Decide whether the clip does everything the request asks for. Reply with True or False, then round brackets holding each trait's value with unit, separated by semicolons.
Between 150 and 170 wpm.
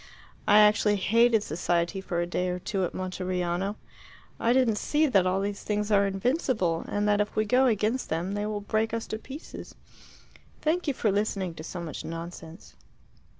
False (185 wpm)